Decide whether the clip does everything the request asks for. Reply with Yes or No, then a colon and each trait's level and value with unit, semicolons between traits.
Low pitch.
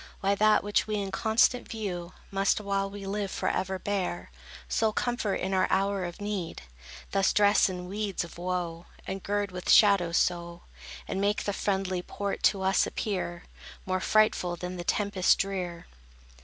No: high, 195 Hz